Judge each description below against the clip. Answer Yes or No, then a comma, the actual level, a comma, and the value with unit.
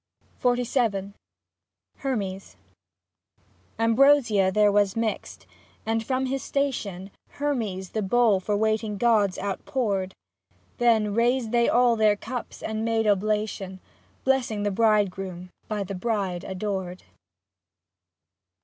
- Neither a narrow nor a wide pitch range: Yes, average, 3.3 semitones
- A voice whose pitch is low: No, high, 215 Hz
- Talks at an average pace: No, slow, 105 wpm